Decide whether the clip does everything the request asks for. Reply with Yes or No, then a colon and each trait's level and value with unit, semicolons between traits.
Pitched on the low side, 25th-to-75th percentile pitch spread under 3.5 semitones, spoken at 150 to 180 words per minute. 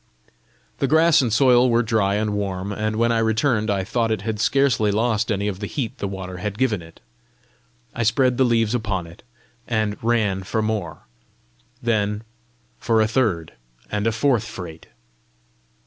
Yes: low, 110 Hz; narrow, 2.5 semitones; average, 170 wpm